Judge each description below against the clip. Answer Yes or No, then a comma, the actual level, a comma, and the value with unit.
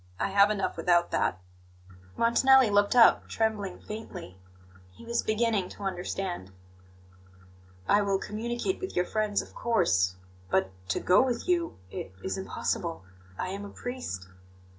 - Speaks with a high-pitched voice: Yes, high, 205 Hz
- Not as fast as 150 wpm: Yes, average, 140 wpm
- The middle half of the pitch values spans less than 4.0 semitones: No, average, 4.7 semitones